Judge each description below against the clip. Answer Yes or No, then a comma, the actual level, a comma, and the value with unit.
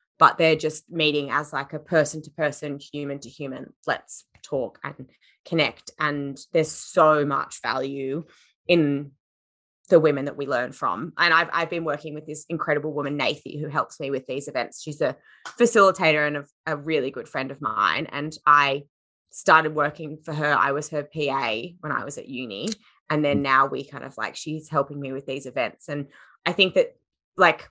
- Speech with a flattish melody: Yes, narrow, 2.0 semitones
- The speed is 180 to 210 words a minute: Yes, average, 195 wpm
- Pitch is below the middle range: No, medium, 150 Hz